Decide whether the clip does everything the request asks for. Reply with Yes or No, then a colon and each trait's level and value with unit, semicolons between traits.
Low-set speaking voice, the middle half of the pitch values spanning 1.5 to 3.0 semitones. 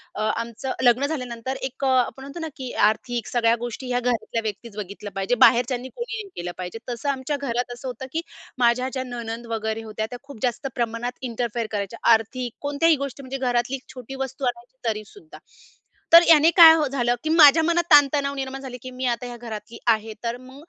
No: high, 245 Hz; average, 2.7 semitones